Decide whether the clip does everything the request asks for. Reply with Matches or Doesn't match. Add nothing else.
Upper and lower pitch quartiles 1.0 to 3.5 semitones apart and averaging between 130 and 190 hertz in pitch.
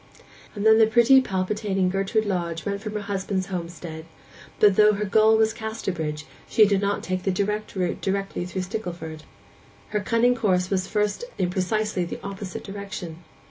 Doesn't match